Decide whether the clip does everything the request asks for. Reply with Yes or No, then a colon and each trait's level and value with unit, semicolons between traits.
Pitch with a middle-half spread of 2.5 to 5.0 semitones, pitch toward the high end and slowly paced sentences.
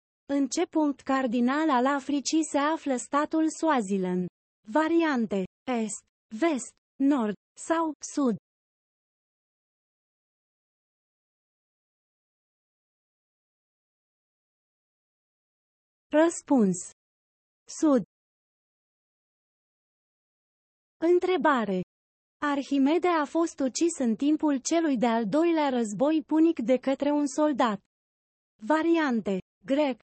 Yes: average, 4.2 semitones; very high, 285 Hz; slow, 70 wpm